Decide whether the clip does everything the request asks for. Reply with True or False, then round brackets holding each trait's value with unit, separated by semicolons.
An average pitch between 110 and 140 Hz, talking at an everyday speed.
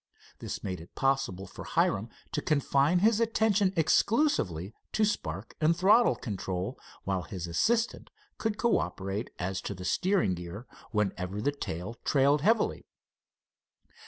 False (135 Hz; 130 wpm)